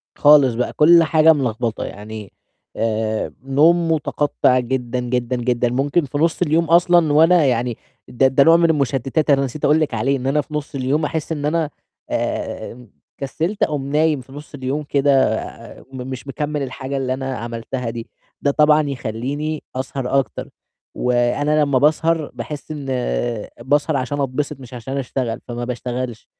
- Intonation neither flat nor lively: Yes, average, 3.3 semitones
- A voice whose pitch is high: No, low, 135 Hz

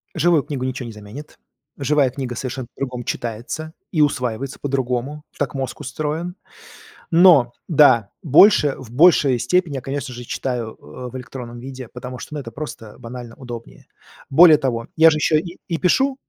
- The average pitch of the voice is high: No, low, 135 Hz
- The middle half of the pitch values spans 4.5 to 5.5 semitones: No, average, 3.8 semitones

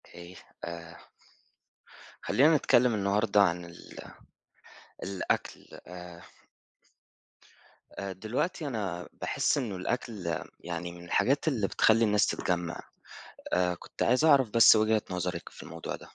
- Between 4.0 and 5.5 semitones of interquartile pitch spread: Yes, average, 4.8 semitones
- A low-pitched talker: Yes, low, 100 Hz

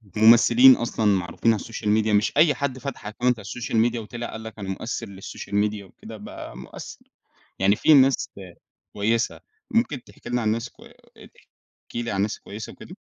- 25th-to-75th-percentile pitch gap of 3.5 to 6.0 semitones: No, average, 2.8 semitones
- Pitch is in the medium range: No, low, 115 Hz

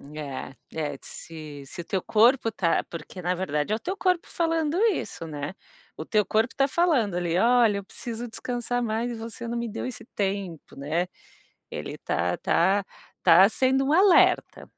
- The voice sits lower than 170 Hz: No, high, 215 Hz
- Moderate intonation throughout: No, wide, 6.0 semitones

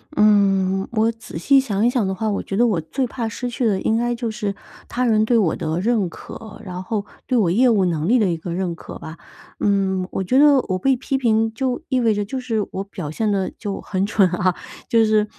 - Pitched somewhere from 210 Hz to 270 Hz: Yes, high, 215 Hz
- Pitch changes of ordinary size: Yes, average, 3.9 semitones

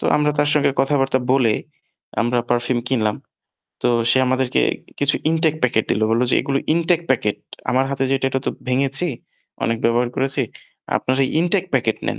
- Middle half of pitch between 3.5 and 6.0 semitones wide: No, average, 2.8 semitones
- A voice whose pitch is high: No, low, 135 Hz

